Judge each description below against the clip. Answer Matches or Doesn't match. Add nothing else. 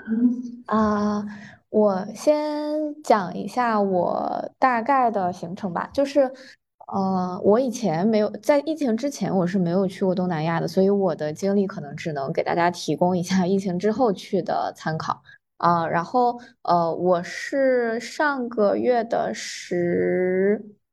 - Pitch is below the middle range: Doesn't match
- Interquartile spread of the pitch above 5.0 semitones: Matches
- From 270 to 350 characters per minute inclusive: Doesn't match